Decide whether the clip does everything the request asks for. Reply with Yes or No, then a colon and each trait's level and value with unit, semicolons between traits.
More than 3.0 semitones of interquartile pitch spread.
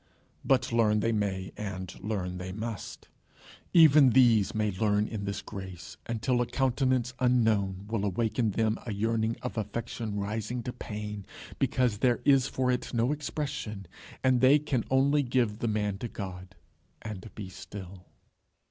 Yes: average, 3.6 semitones